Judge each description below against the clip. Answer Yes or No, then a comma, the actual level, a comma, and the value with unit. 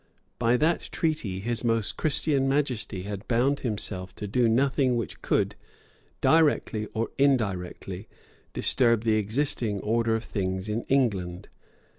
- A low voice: Yes, low, 115 Hz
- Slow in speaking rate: Yes, slow, 130 wpm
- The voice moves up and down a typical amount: Yes, average, 4.7 semitones